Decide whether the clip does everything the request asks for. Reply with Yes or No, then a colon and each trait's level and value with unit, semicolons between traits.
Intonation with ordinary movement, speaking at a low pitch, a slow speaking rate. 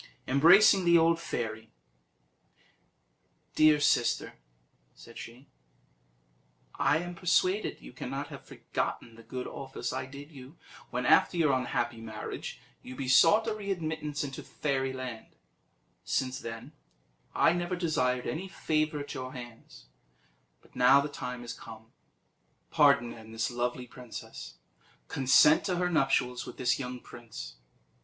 Yes: average, 4.8 semitones; low, 130 Hz; slow, 130 wpm